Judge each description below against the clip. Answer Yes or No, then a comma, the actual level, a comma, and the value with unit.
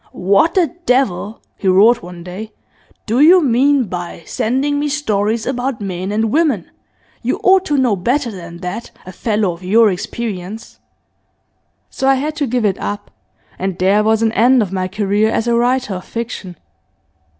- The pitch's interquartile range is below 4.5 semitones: No, average, 5.3 semitones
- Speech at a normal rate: Yes, average, 170 wpm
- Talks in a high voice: Yes, high, 220 Hz